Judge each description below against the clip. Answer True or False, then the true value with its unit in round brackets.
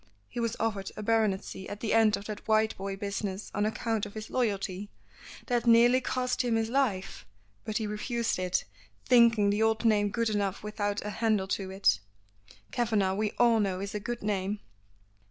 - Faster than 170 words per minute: True (180 wpm)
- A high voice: True (215 Hz)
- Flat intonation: True (2.2 semitones)